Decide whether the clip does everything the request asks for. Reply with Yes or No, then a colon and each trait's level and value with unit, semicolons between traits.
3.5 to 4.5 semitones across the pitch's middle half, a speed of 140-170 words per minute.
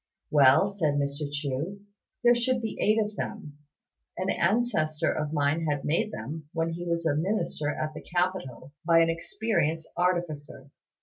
Yes: average, 4.2 semitones; average, 160 wpm